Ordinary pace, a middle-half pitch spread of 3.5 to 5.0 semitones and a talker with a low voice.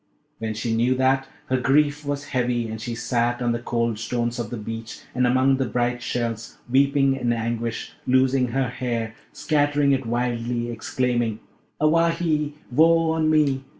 No: average, 160 wpm; average, 2.8 semitones; low, 125 Hz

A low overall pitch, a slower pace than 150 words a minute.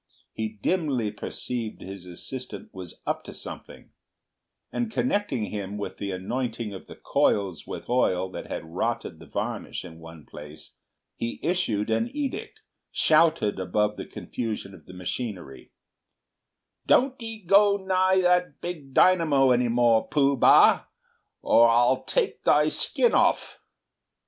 Yes: low, 120 Hz; average, 140 wpm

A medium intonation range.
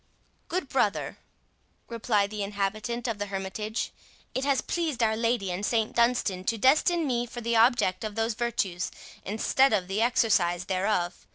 Yes: average, 3.2 semitones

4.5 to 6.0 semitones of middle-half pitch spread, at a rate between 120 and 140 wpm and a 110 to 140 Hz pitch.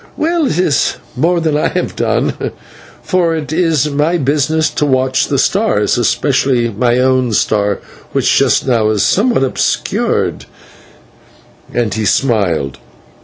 Yes: average, 5.2 semitones; slow, 135 wpm; low, 135 Hz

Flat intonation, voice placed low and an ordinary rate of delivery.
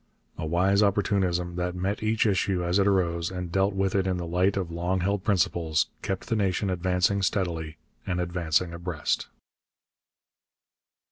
Yes: narrow, 2.0 semitones; very low, 90 Hz; average, 155 wpm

